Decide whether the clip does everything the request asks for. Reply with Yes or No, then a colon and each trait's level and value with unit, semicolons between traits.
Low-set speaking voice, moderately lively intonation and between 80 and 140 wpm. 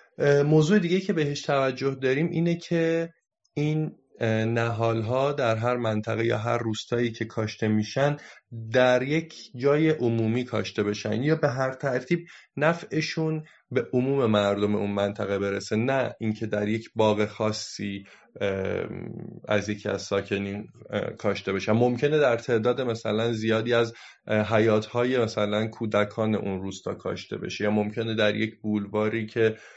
Yes: low, 115 Hz; average, 4.1 semitones; average, 135 wpm